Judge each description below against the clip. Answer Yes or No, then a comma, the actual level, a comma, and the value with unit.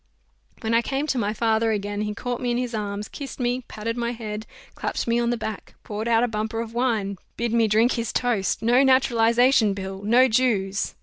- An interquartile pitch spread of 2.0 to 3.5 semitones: Yes, narrow, 2.4 semitones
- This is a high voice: Yes, high, 230 Hz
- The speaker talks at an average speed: No, fast, 210 wpm